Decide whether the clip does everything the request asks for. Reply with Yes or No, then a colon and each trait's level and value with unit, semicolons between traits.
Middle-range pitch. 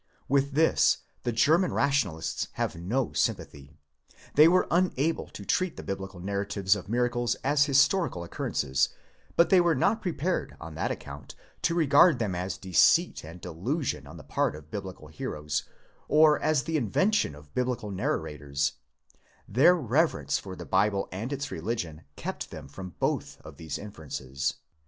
No: low, 110 Hz